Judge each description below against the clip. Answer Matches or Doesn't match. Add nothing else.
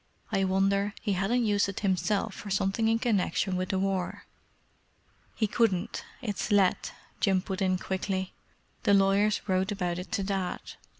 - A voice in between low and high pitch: Doesn't match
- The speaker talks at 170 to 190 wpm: Doesn't match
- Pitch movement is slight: Matches